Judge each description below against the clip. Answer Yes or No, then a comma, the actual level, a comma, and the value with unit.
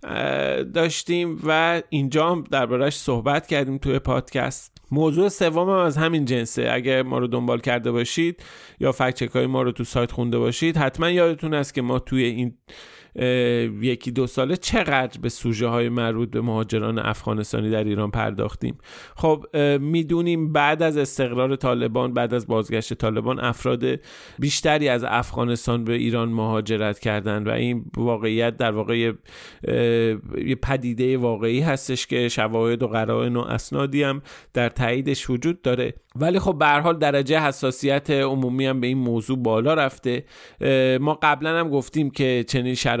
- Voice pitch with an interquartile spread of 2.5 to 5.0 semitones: Yes, average, 3.6 semitones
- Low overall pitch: Yes, low, 125 Hz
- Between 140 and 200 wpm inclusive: Yes, average, 150 wpm